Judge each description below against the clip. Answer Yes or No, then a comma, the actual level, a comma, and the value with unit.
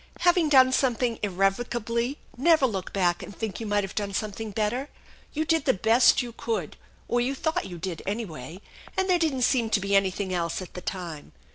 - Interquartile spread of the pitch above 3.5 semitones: Yes, average, 5.1 semitones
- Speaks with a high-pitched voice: Yes, high, 220 Hz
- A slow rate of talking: No, average, 195 wpm